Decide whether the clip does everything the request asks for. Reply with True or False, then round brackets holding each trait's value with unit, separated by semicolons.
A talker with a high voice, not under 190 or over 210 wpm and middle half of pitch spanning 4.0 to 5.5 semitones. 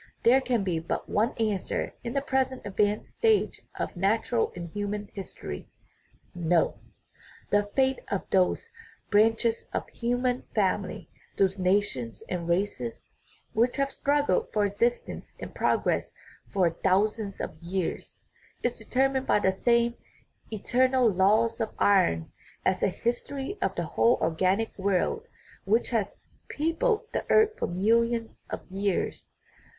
False (215 Hz; 140 wpm; 4.4 semitones)